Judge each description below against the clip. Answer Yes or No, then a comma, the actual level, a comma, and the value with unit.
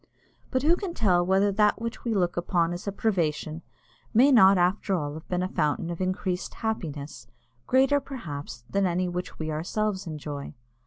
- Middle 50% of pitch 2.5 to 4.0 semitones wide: No, average, 4.4 semitones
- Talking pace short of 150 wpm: No, average, 170 wpm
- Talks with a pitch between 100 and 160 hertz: No, medium, 185 Hz